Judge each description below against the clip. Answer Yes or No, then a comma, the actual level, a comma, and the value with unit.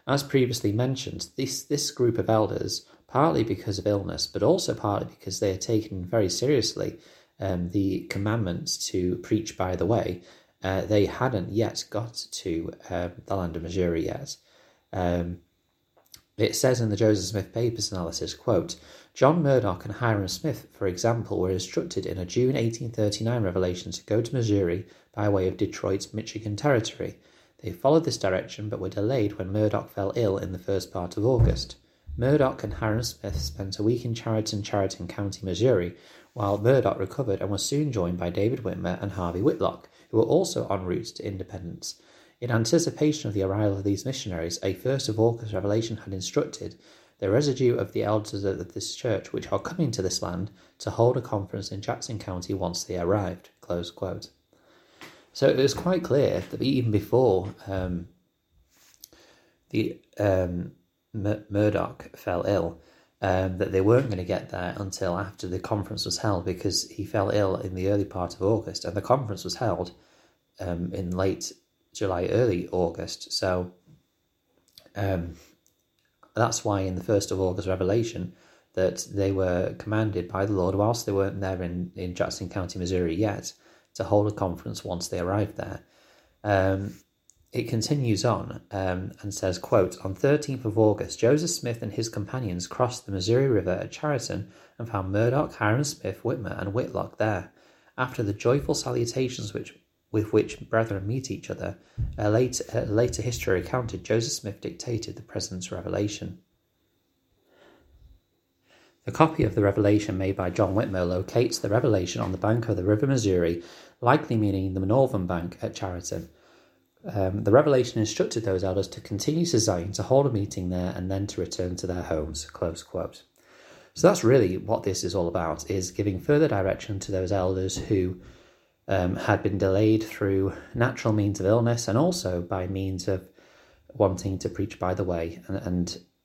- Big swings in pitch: No, average, 3.6 semitones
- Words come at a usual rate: Yes, average, 170 wpm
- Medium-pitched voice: No, low, 100 Hz